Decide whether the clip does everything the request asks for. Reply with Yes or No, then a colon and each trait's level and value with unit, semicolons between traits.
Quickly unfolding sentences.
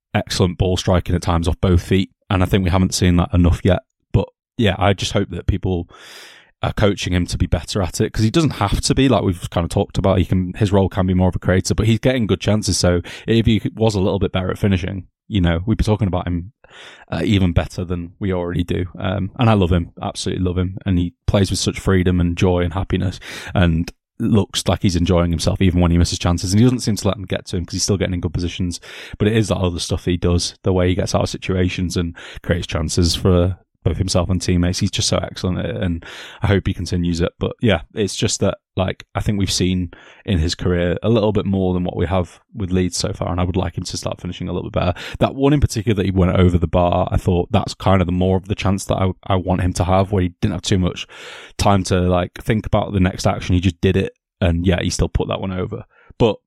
Yes: fast, 270 wpm